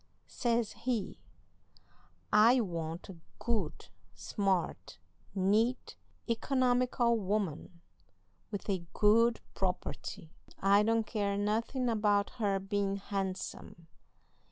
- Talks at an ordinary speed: No, slow, 90 wpm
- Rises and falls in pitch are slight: No, average, 3.1 semitones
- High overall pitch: Yes, high, 205 Hz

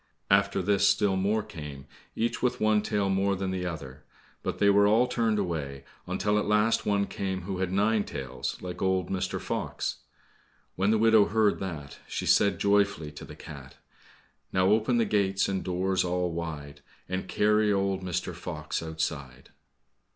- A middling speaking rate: Yes, average, 170 wpm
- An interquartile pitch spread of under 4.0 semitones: Yes, average, 2.8 semitones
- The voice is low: Yes, very low, 95 Hz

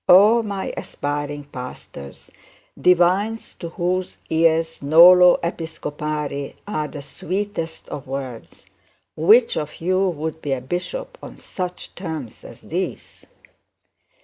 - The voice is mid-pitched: Yes, medium, 165 Hz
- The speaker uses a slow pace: Yes, slow, 115 wpm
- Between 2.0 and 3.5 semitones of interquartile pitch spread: No, average, 4.0 semitones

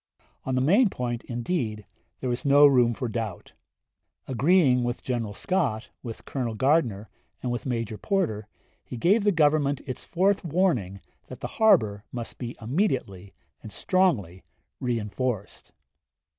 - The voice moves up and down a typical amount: No, wide, 5.9 semitones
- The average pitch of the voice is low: Yes, low, 125 Hz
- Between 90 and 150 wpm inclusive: Yes, average, 140 wpm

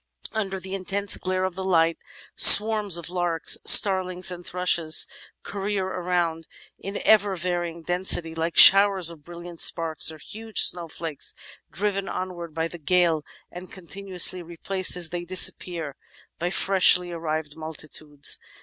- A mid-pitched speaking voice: Yes, medium, 175 Hz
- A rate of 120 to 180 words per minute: Yes, slow, 135 wpm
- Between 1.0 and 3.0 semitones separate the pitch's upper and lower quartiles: Yes, narrow, 2.4 semitones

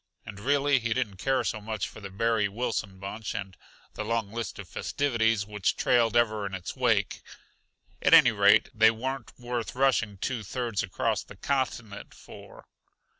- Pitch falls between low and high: No, low, 110 Hz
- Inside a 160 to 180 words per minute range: Yes, average, 170 wpm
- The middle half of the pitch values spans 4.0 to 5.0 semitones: No, average, 3.3 semitones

